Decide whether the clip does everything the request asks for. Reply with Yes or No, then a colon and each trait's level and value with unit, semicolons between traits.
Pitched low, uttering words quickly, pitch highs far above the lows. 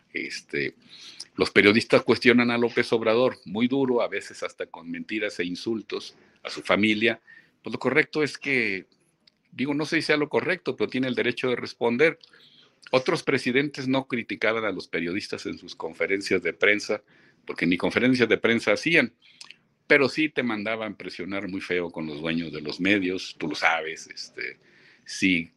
No: low, 115 Hz; average, 170 wpm; wide, 6.3 semitones